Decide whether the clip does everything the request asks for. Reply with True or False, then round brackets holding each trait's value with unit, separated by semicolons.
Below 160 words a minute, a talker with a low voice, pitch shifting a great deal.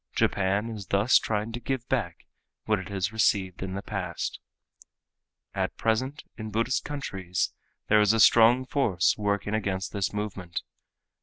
False (150 wpm; 105 Hz; 2.9 semitones)